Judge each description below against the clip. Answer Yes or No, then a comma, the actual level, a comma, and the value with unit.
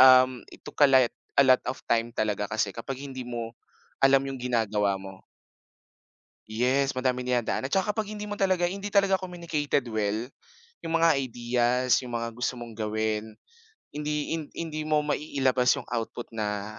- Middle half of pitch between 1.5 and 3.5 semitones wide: No, average, 4.6 semitones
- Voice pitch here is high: No, low, 125 Hz